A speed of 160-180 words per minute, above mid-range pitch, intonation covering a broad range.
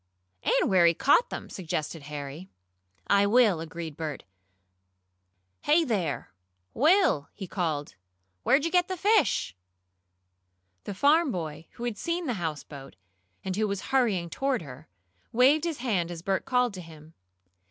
No: average, 145 wpm; high, 195 Hz; wide, 8.8 semitones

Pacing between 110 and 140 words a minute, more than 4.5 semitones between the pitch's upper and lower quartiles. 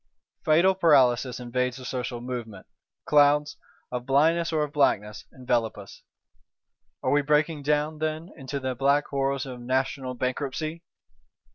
No: slow, 135 wpm; average, 3.1 semitones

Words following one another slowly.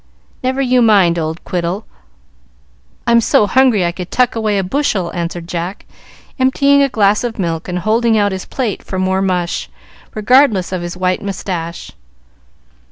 No: average, 160 wpm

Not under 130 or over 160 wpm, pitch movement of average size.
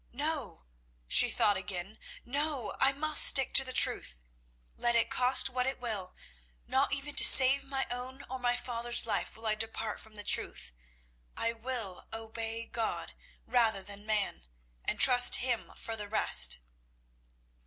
Yes: average, 155 wpm; average, 3.3 semitones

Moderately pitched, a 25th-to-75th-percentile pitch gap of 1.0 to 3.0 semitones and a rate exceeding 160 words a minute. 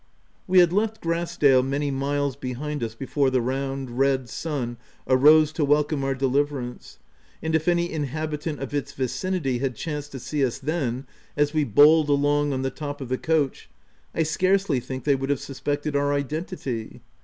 Yes: medium, 145 Hz; narrow, 2.6 semitones; average, 180 wpm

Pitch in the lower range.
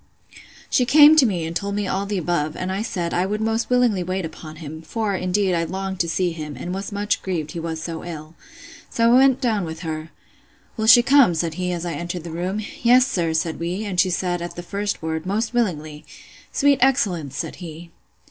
No: medium, 185 Hz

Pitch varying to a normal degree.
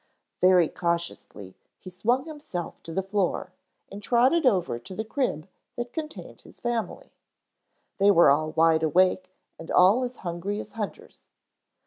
No: wide, 5.8 semitones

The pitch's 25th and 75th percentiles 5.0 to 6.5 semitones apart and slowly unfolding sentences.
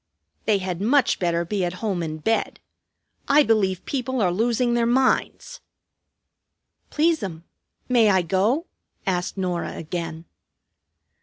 Yes: wide, 5.4 semitones; slow, 125 wpm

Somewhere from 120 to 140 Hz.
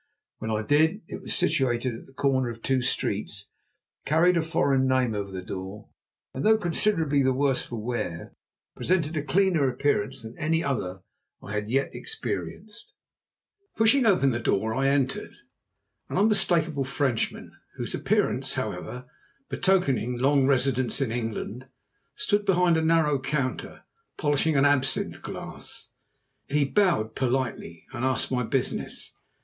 Yes: low, 135 Hz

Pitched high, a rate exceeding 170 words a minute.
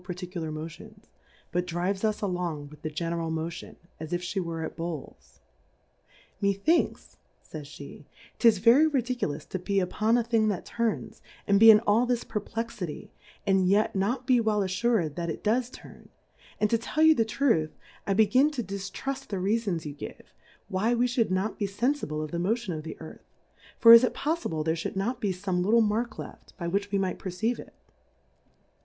Yes: high, 200 Hz; average, 190 wpm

